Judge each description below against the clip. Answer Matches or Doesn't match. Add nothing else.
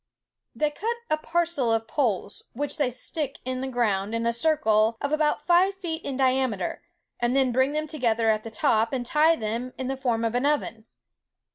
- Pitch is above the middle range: Matches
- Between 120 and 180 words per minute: Doesn't match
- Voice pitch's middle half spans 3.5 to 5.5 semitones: Matches